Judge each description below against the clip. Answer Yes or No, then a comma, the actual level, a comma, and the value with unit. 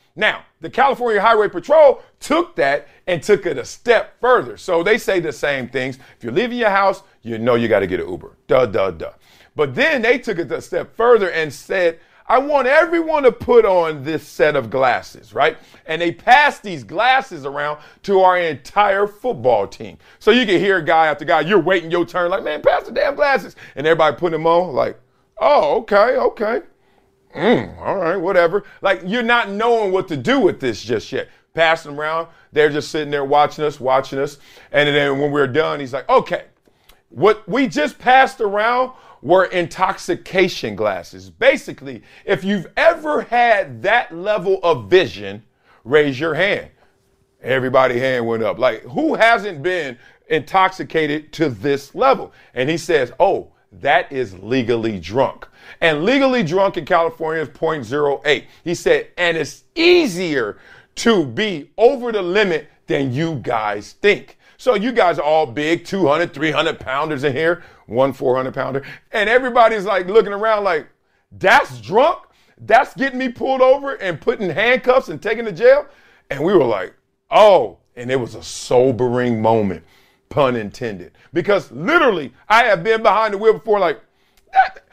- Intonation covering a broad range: Yes, wide, 8.2 semitones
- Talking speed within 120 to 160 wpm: No, average, 170 wpm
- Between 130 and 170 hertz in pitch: No, medium, 180 Hz